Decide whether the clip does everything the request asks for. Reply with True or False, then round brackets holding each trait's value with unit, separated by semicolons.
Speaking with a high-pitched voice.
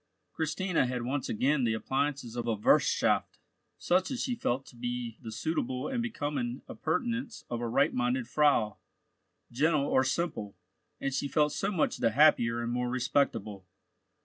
False (130 Hz)